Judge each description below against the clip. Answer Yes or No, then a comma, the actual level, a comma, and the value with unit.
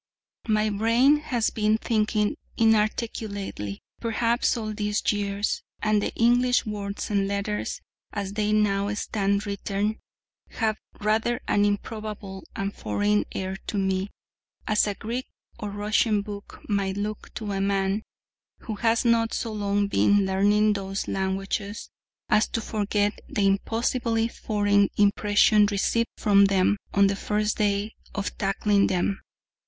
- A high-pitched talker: Yes, high, 205 Hz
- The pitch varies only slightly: Yes, narrow, 1.4 semitones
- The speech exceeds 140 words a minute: No, slow, 135 wpm